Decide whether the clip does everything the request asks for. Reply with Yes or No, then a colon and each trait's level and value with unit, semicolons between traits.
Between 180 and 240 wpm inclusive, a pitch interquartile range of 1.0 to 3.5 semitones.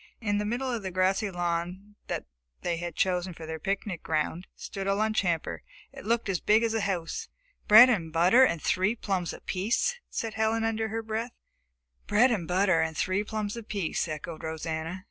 No: average, 185 wpm; average, 4.2 semitones